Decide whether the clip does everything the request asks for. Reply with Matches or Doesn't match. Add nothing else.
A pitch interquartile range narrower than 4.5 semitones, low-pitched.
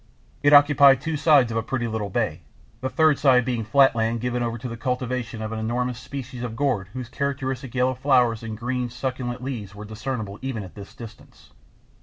Matches